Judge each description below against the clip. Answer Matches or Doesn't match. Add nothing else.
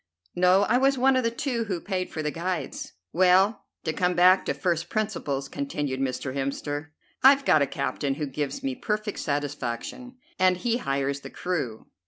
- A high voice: Doesn't match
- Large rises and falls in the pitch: Matches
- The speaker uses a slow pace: Doesn't match